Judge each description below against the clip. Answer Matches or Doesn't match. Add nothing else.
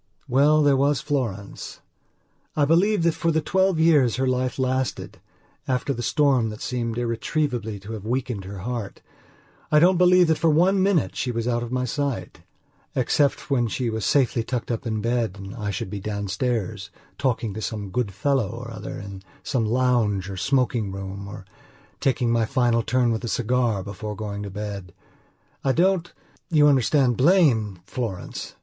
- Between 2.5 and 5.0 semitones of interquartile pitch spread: Matches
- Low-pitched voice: Matches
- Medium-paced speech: Matches